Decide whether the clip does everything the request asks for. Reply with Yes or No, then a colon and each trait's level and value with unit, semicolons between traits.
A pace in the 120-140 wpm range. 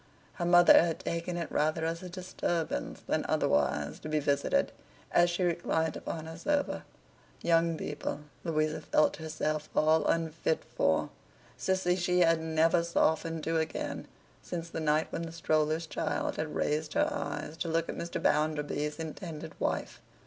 No: average, 155 wpm